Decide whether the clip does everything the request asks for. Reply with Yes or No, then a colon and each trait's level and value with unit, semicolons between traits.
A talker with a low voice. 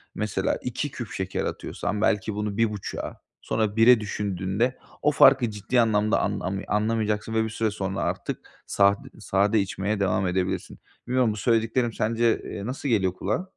Yes: low, 105 Hz